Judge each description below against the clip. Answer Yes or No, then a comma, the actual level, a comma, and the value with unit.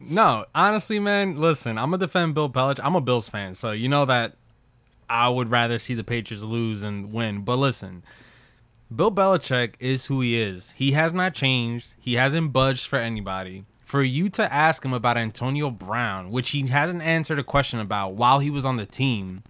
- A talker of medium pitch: No, low, 125 Hz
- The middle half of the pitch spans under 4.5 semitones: Yes, average, 3.8 semitones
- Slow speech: No, average, 200 wpm